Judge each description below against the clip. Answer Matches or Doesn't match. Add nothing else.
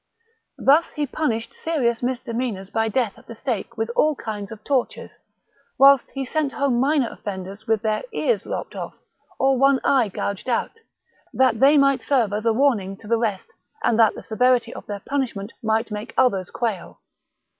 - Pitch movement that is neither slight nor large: Matches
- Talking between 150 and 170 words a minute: Doesn't match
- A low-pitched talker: Doesn't match